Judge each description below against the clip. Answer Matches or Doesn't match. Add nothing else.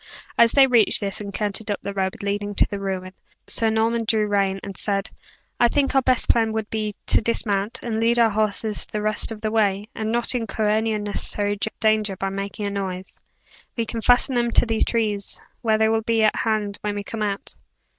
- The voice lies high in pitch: Matches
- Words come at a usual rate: Doesn't match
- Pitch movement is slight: Matches